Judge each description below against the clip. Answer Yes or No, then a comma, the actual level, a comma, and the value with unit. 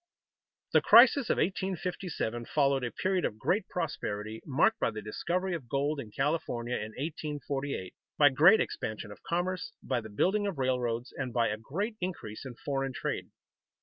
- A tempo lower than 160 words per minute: No, average, 165 wpm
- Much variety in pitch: Yes, wide, 7.2 semitones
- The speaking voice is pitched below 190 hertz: Yes, medium, 140 Hz